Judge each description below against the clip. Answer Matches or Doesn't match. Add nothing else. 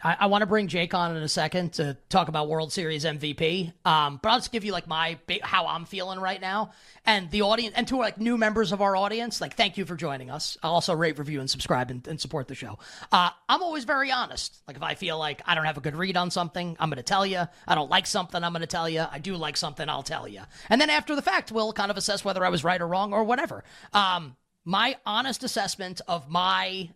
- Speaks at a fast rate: Matches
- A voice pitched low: Doesn't match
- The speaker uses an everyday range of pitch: Matches